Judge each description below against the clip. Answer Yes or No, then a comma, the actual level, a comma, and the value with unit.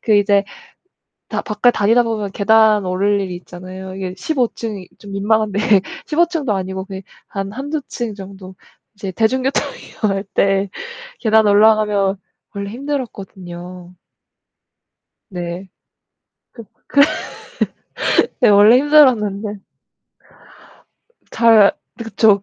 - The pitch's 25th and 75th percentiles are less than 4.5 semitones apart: Yes, narrow, 2.6 semitones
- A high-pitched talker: Yes, high, 205 Hz